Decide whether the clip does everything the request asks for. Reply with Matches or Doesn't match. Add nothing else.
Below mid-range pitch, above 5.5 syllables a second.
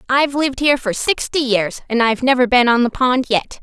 Doesn't match